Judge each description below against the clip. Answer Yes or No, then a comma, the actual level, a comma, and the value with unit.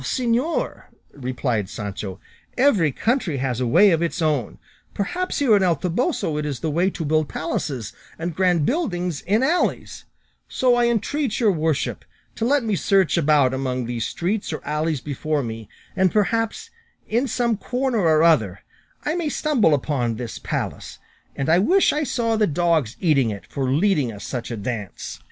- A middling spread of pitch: No, wide, 8.9 semitones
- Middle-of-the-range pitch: Yes, medium, 165 Hz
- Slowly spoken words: No, average, 175 wpm